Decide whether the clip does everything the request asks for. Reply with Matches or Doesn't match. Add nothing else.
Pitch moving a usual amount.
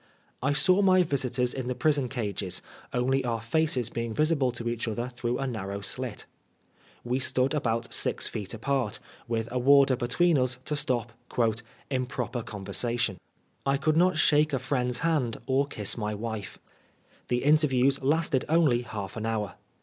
Matches